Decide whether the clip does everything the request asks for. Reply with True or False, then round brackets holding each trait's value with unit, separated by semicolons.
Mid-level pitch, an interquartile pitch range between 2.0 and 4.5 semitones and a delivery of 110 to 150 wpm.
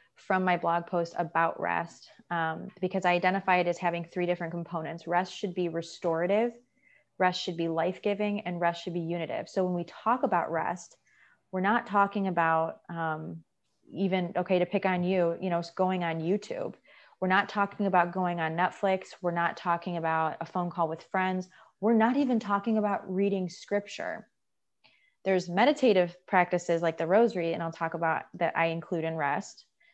False (180 Hz; 2.5 semitones; 180 wpm)